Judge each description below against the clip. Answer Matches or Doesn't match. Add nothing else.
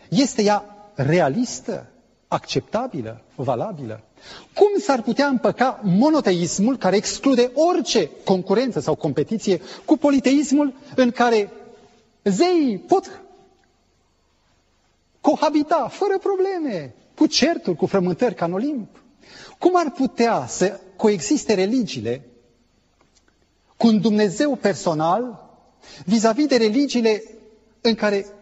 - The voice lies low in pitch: Doesn't match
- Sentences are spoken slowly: Matches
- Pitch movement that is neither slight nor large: Doesn't match